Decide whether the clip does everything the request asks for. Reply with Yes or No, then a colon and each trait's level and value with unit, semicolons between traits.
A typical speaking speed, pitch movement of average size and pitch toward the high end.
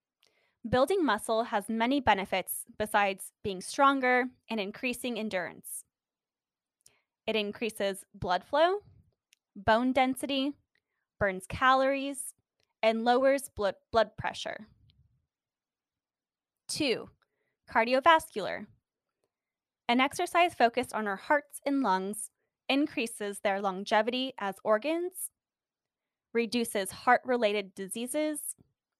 No: slow, 85 wpm; average, 4.9 semitones; high, 235 Hz